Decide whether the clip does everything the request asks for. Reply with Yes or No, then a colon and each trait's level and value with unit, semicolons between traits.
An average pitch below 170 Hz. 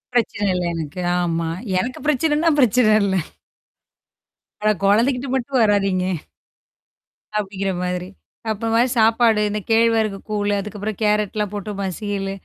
No: high, 210 Hz